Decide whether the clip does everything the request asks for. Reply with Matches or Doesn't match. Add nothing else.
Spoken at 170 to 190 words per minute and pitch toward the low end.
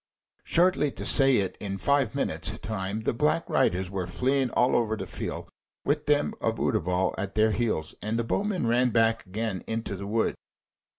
Matches